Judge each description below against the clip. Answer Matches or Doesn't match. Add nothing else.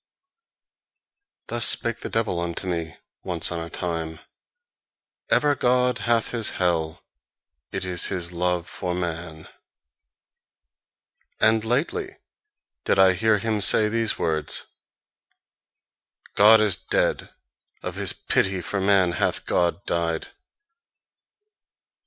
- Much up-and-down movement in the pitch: Doesn't match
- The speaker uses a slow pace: Matches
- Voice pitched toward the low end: Matches